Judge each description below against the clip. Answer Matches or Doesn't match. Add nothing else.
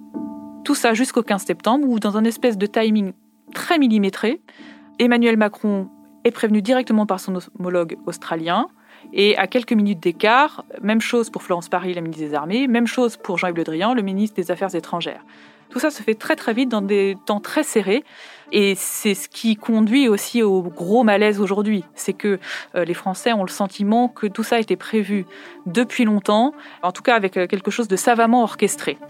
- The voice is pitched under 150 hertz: Doesn't match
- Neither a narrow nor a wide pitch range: Matches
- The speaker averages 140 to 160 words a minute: Doesn't match